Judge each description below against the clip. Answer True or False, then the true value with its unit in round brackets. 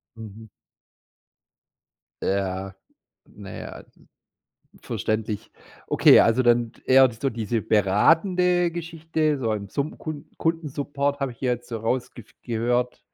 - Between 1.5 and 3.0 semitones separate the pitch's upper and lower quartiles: False (5.0 semitones)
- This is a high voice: False (125 Hz)